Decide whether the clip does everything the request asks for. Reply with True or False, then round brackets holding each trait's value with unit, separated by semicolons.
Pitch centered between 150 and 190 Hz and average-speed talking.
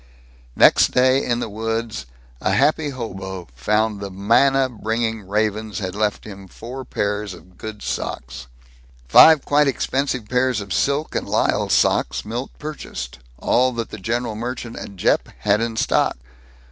False (110 Hz; 155 wpm)